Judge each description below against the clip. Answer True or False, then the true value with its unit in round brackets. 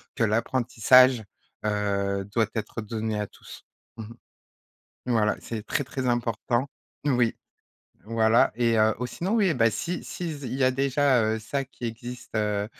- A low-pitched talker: True (115 Hz)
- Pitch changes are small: False (3.0 semitones)